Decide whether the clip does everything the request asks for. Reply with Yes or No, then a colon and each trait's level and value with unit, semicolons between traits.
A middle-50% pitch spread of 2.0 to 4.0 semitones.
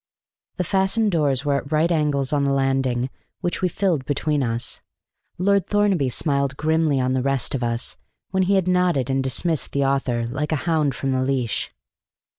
No: average, 4.4 semitones